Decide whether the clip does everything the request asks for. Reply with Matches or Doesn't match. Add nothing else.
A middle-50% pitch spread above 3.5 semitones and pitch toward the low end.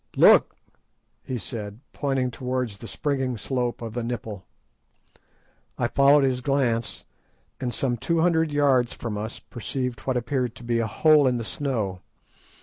Doesn't match